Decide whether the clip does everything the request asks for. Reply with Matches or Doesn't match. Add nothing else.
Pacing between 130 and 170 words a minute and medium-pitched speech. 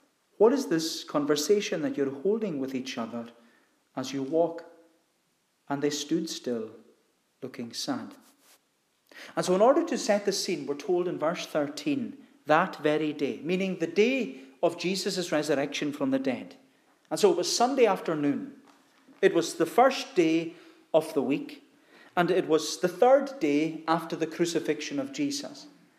Matches